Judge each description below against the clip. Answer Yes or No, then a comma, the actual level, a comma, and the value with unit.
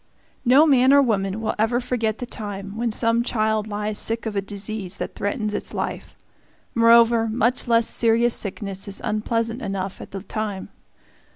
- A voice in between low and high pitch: No, high, 220 Hz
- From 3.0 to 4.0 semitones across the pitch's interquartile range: No, narrow, 2.4 semitones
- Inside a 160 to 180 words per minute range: Yes, average, 170 wpm